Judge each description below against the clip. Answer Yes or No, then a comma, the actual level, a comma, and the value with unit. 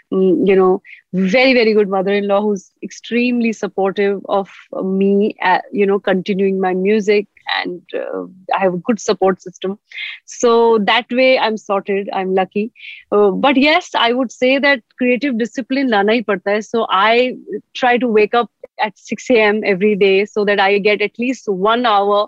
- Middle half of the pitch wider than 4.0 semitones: No, average, 3.3 semitones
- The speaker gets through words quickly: No, average, 165 wpm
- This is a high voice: Yes, high, 210 Hz